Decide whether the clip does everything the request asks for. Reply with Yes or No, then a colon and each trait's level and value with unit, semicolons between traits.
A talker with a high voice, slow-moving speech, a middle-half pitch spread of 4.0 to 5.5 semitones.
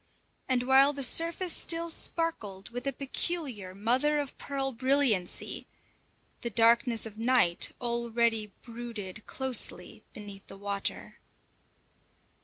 Yes: high, 240 Hz; slow, 110 wpm; average, 4.3 semitones